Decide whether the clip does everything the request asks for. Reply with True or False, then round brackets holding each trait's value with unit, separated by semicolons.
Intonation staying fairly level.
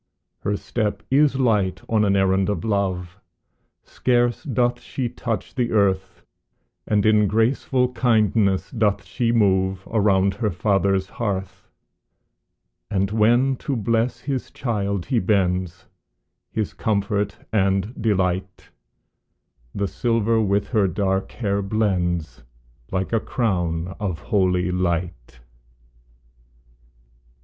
False (3.2 semitones)